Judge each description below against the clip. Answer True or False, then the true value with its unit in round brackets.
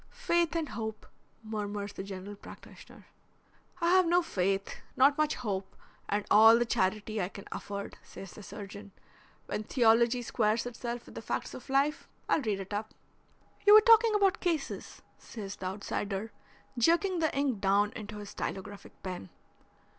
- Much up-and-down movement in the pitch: True (6.1 semitones)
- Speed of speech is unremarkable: True (160 wpm)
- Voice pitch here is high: True (220 Hz)